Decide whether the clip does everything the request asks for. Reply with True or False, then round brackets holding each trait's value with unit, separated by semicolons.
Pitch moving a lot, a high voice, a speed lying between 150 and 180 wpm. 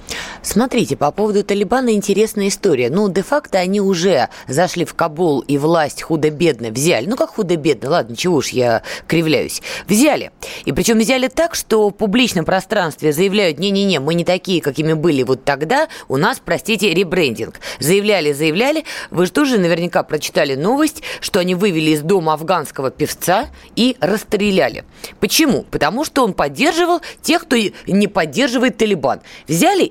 True (6.0 semitones; 195 Hz; 155 wpm)